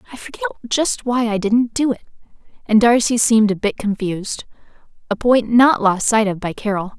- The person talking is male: No, female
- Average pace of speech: Yes, average, 190 wpm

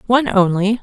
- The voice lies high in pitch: Yes, high, 215 Hz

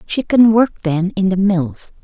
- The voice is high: Yes, high, 195 Hz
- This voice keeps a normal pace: Yes, average, 175 wpm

